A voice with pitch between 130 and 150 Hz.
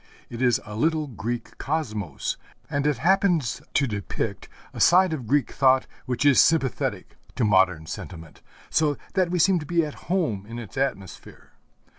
Yes: low, 135 Hz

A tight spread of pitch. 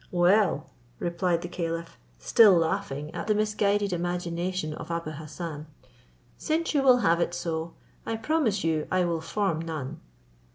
No: average, 3.6 semitones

